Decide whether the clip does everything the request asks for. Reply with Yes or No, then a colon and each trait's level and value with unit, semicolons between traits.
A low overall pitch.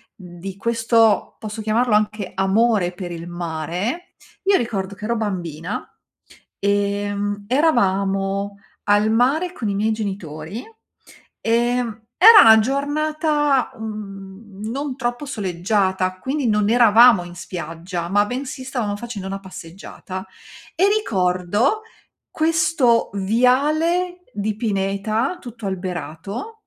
No: high, 210 Hz